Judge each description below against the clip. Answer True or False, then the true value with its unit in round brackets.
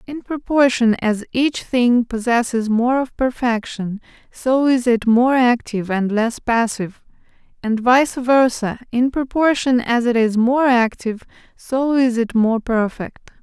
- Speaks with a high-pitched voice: True (240 Hz)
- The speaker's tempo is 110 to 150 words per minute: True (145 wpm)